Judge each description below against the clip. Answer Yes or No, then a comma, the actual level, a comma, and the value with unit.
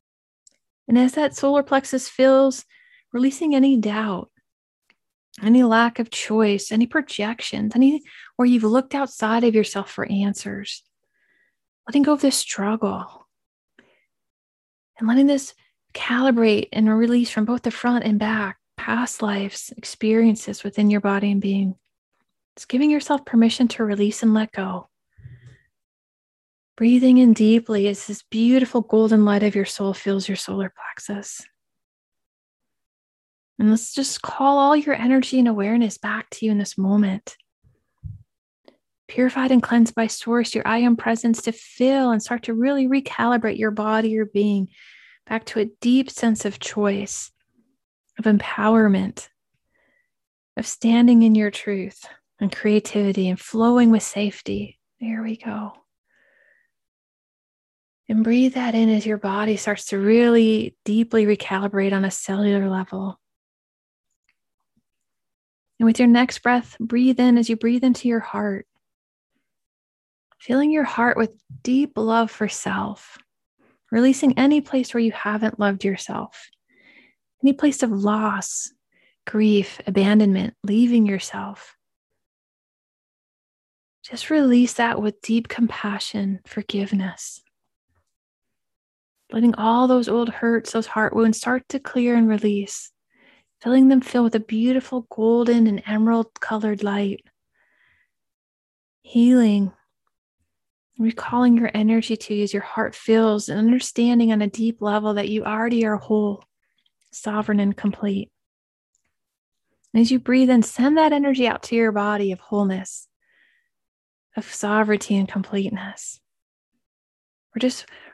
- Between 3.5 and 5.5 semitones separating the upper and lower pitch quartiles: No, average, 2.9 semitones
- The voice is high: Yes, high, 225 Hz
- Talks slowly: Yes, slow, 130 wpm